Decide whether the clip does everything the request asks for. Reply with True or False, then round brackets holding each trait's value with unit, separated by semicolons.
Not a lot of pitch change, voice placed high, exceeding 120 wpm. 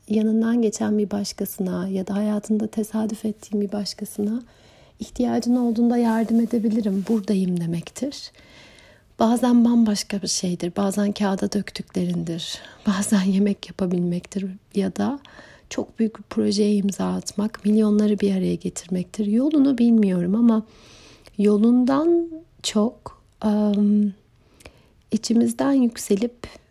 False (2.3 semitones; 210 Hz; 105 wpm)